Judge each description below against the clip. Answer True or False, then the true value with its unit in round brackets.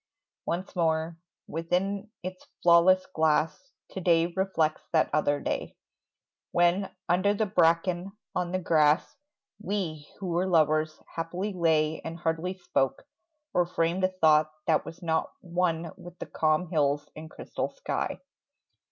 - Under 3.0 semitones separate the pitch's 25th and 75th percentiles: True (2.6 semitones)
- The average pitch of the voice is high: False (170 Hz)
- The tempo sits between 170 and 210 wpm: False (135 wpm)